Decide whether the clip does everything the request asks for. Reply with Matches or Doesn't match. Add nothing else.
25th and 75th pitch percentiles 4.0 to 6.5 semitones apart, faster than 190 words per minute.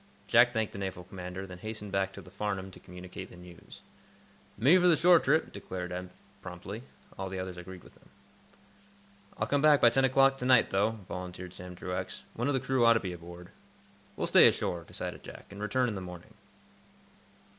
Matches